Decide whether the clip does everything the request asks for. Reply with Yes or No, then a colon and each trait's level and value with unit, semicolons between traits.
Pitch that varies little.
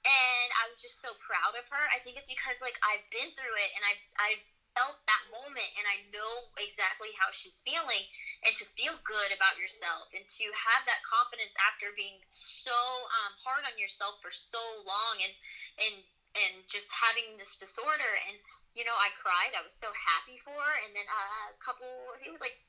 No: average, 3.8 semitones